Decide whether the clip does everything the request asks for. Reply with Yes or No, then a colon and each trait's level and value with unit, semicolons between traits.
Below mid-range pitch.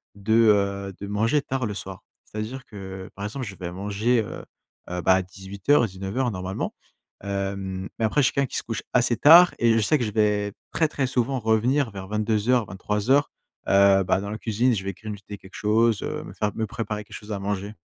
Yes: low, 105 Hz